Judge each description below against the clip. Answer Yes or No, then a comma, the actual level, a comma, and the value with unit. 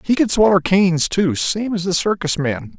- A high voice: No, medium, 180 Hz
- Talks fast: Yes, fast, 215 wpm